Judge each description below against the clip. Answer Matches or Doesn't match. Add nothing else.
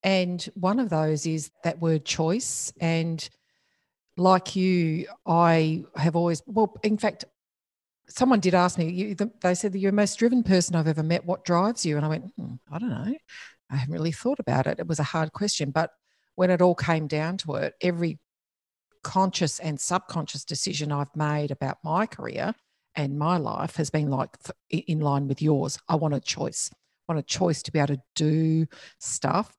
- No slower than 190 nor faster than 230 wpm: Matches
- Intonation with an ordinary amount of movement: Matches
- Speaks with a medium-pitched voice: Matches